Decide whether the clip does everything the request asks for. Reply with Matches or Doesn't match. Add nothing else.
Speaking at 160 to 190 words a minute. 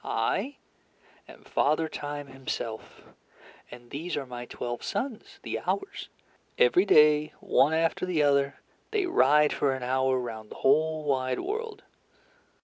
Doesn't match